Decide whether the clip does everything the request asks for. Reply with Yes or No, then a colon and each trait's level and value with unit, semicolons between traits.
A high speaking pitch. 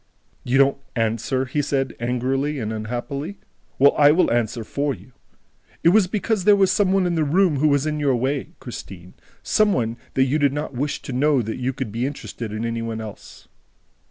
No: low, 135 Hz